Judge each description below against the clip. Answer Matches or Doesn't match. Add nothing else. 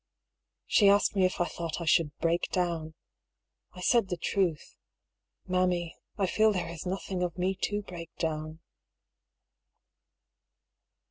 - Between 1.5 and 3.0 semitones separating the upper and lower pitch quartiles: Matches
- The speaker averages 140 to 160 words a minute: Matches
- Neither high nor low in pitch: Matches